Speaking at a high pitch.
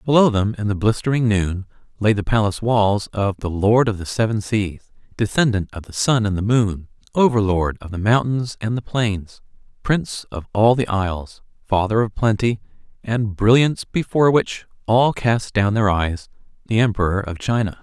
No: low, 105 Hz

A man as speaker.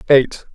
Yes: male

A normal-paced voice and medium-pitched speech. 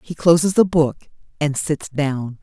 Yes: average, 175 wpm; medium, 155 Hz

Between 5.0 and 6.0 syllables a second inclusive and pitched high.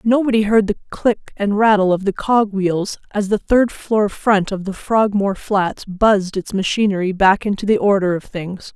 No: 4.7 syllables/s; high, 200 Hz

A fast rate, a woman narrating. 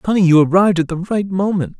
No: fast, 235 wpm; male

